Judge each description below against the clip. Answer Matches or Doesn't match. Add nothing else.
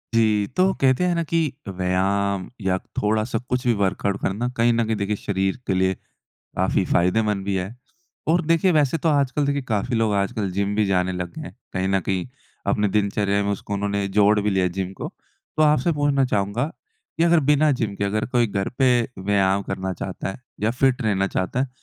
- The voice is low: Matches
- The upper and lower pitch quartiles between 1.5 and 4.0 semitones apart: Doesn't match